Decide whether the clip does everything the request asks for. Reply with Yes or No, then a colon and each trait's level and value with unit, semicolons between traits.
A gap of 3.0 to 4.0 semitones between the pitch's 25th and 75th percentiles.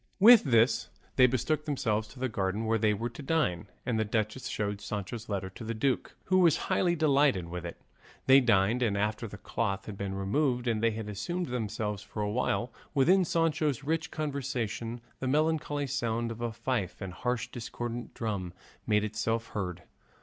No: average, 4.5 semitones